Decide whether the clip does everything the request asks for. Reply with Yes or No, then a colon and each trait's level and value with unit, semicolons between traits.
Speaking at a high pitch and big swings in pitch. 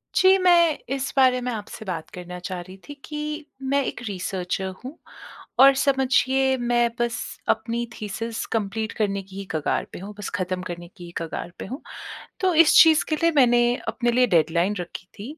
Yes: high, 230 Hz; wide, 6.0 semitones